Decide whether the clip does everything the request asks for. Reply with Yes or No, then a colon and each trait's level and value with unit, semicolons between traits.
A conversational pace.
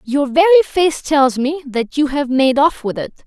No: fast, 220 wpm